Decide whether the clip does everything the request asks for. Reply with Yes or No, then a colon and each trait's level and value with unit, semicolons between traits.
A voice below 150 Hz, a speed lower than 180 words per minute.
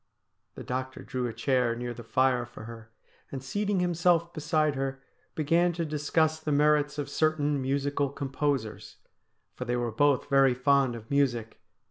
Yes: medium, 140 Hz; average, 160 wpm